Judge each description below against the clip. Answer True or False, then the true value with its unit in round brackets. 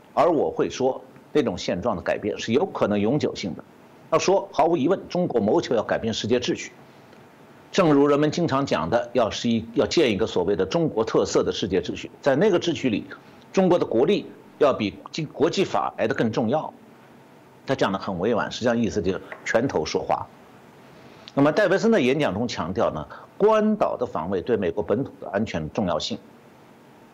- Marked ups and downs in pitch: True (8.5 semitones)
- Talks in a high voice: False (140 Hz)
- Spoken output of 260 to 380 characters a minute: True (285 characters per minute)